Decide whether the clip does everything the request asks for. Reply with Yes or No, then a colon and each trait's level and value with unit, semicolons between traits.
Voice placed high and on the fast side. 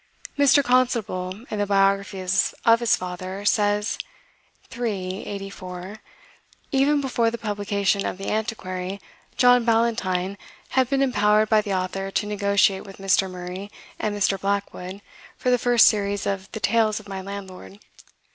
No: high, 205 Hz; average, 145 wpm